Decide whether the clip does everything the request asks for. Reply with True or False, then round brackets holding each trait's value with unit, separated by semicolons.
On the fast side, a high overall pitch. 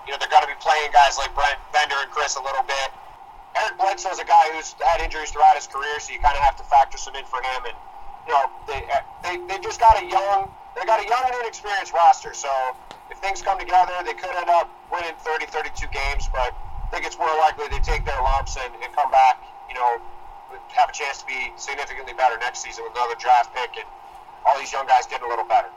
True (245 wpm; 210 Hz)